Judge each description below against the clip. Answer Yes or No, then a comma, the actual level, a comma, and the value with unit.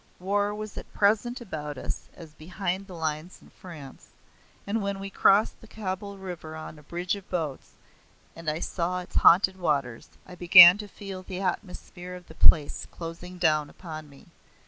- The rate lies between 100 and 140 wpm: No, average, 175 wpm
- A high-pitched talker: No, medium, 180 Hz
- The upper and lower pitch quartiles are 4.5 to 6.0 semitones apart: No, average, 3.7 semitones